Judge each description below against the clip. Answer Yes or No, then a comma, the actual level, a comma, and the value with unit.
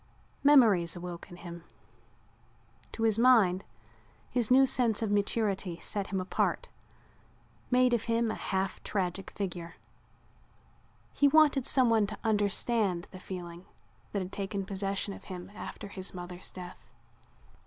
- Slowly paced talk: Yes, slow, 130 wpm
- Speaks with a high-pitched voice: Yes, high, 200 Hz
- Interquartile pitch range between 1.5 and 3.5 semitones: No, average, 3.9 semitones